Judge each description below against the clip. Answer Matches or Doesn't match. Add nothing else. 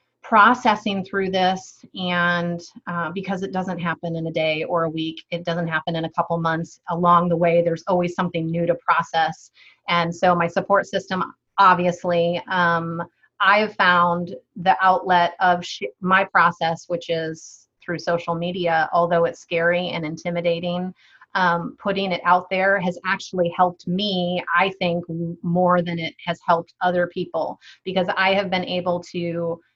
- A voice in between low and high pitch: Matches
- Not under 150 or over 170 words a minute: Matches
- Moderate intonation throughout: Doesn't match